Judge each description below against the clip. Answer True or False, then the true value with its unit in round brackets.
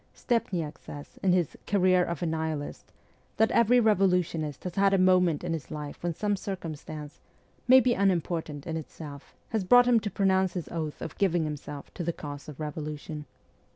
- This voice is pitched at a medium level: True (170 Hz)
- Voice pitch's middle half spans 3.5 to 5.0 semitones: True (4.2 semitones)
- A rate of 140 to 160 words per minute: False (180 wpm)